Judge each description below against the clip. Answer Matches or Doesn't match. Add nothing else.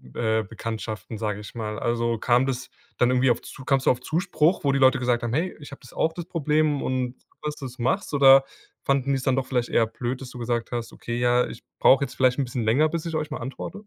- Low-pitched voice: Matches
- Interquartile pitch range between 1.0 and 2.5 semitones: Doesn't match